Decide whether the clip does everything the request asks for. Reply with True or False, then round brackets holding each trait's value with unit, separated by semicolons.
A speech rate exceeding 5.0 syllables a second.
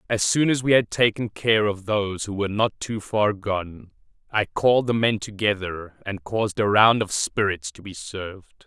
False (4.8 syllables/s)